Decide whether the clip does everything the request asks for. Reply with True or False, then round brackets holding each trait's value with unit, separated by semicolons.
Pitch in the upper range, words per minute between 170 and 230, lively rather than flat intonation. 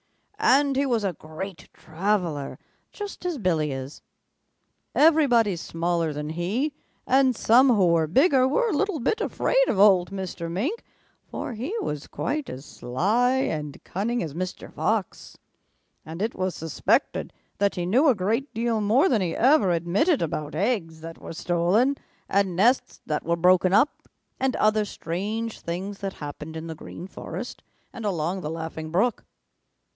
False (195 Hz; 160 wpm; 6.7 semitones)